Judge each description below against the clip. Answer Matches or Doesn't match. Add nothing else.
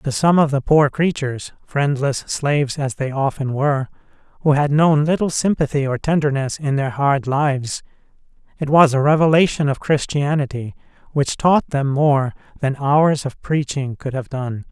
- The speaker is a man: Matches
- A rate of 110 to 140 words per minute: Doesn't match